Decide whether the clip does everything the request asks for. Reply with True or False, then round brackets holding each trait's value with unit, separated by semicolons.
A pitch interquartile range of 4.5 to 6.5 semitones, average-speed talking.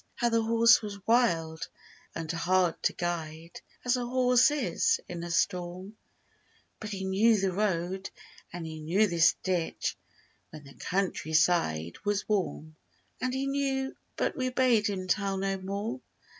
True (5.2 semitones; 150 wpm)